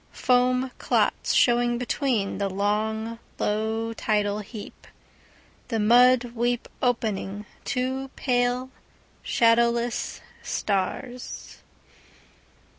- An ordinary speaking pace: No, slow, 70 wpm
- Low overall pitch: No, high, 235 Hz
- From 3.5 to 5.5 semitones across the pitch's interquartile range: No, narrow, 2.6 semitones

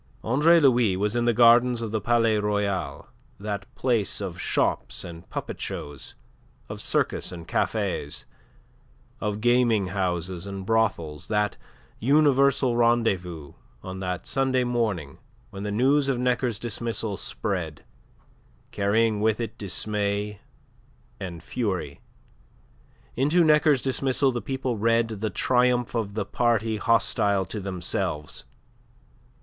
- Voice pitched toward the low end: Yes, low, 110 Hz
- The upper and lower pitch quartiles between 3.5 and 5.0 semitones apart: Yes, average, 3.9 semitones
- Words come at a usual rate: No, slow, 120 wpm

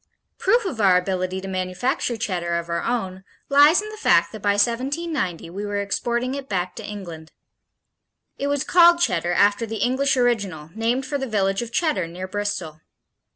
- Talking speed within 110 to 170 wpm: No, average, 180 wpm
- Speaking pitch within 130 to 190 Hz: No, high, 205 Hz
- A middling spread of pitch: No, wide, 6.1 semitones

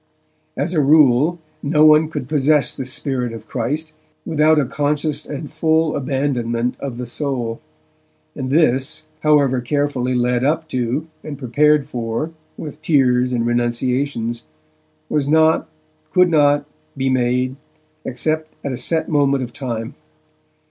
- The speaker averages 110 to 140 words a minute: Yes, slow, 135 wpm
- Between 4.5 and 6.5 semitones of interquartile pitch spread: No, average, 3.5 semitones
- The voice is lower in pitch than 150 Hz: Yes, medium, 140 Hz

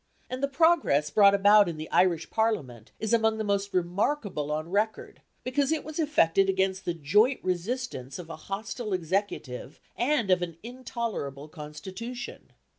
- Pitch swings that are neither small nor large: No, wide, 6.1 semitones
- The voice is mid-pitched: No, high, 200 Hz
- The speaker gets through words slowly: No, average, 155 wpm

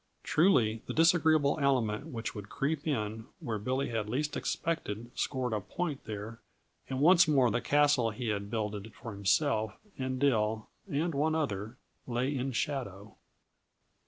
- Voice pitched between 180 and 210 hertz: No, low, 125 Hz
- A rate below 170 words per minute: Yes, average, 150 wpm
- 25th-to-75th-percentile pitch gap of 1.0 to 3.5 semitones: No, average, 5.2 semitones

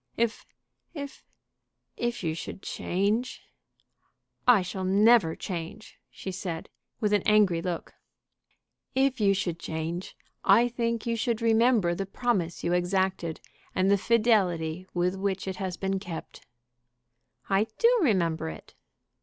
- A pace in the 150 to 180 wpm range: No, slow, 135 wpm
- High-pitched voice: Yes, high, 195 Hz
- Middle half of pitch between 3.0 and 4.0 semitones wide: No, average, 4.4 semitones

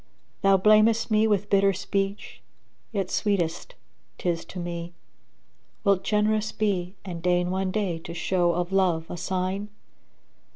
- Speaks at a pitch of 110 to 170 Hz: No, high, 190 Hz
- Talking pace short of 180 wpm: Yes, average, 140 wpm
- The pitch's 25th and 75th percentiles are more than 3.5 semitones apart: No, average, 2.8 semitones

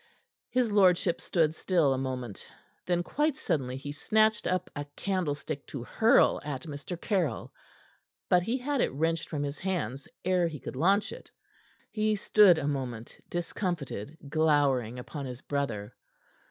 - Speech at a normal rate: Yes, average, 150 wpm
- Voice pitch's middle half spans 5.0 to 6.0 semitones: Yes, average, 5.3 semitones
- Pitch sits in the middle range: Yes, medium, 160 Hz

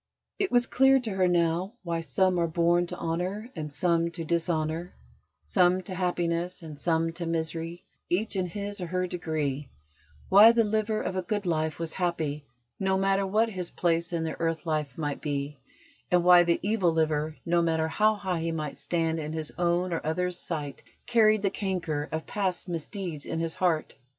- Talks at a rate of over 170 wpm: Yes, average, 190 wpm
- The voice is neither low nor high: Yes, medium, 170 Hz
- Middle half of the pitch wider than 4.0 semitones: No, average, 2.7 semitones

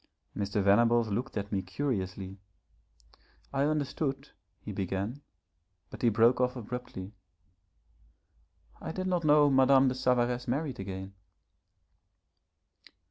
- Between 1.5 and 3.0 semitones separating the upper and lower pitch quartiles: No, average, 5.3 semitones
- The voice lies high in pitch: No, low, 125 Hz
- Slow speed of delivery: Yes, slow, 110 wpm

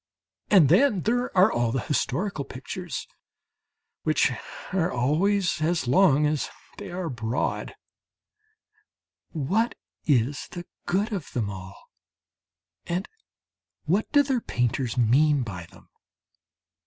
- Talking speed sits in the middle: No, slow, 115 wpm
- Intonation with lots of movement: Yes, wide, 7.2 semitones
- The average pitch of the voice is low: No, medium, 155 Hz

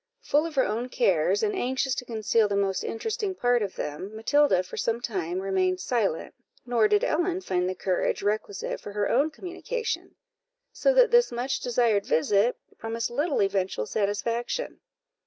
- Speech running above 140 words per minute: Yes, average, 165 wpm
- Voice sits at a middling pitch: No, high, 230 Hz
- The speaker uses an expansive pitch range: Yes, wide, 6.8 semitones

